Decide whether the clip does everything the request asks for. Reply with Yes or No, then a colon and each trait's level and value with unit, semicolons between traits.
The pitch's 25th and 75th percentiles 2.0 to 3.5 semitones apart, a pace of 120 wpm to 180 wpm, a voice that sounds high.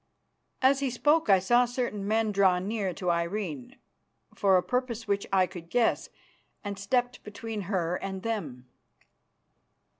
No: average, 4.2 semitones; average, 145 wpm; high, 205 Hz